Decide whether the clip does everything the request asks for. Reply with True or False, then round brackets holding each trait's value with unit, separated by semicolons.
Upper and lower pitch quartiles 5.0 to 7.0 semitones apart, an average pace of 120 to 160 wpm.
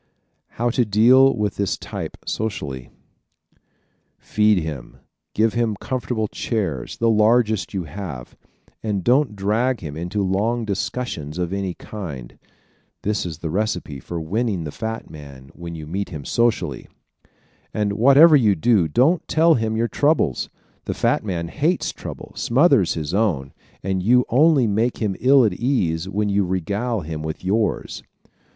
True (5.6 semitones; 155 wpm)